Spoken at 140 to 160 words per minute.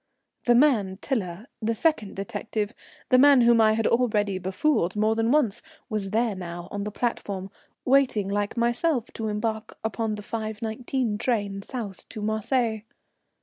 Yes: average, 150 wpm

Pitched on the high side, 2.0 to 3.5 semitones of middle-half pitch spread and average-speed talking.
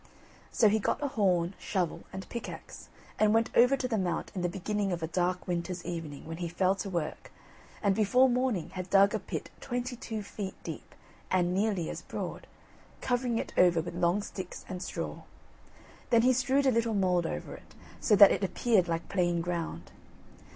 No: high, 195 Hz; average, 4.4 semitones; average, 190 wpm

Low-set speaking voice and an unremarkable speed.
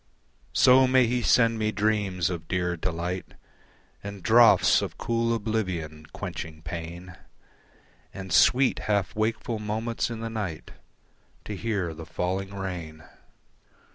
No: low, 100 Hz; slow, 125 wpm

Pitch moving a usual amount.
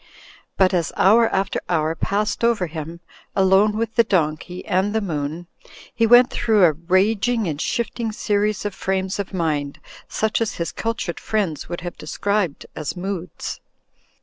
Yes: average, 4.1 semitones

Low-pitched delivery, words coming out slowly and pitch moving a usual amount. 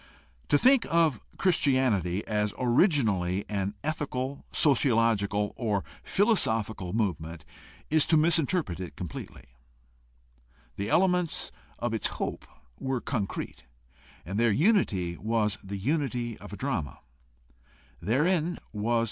No: low, 115 Hz; slow, 120 wpm; wide, 6.9 semitones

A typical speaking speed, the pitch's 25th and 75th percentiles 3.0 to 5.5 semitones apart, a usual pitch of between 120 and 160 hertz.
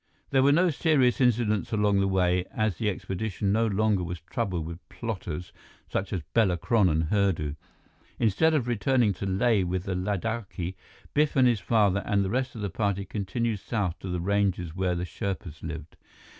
No: average, 185 wpm; average, 4.0 semitones; low, 100 Hz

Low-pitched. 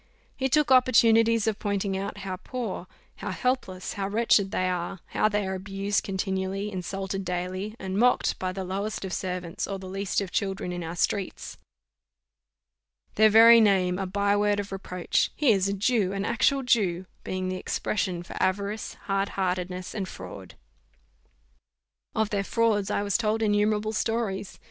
No: high, 200 Hz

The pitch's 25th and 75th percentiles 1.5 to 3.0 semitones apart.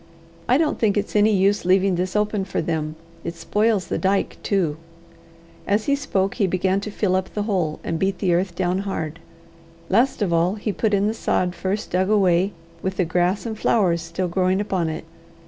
Yes: average, 2.7 semitones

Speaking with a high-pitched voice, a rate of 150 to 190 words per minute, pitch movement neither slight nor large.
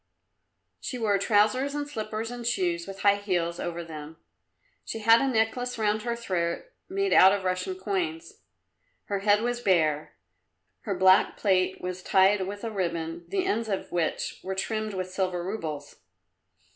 Yes: high, 195 Hz; average, 160 wpm; average, 3.7 semitones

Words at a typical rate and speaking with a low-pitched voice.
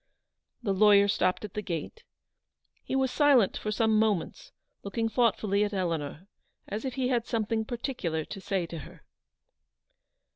No: average, 150 wpm; high, 210 Hz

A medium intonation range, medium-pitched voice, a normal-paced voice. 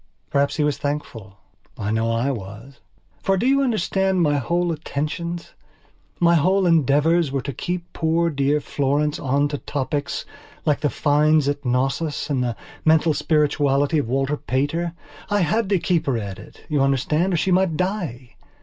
Yes: average, 3.8 semitones; medium, 150 Hz; average, 170 wpm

